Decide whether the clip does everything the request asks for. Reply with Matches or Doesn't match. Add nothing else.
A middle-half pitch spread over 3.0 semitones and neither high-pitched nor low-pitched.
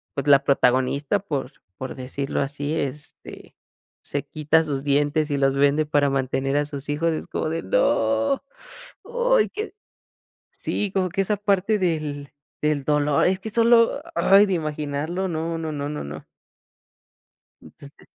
Matches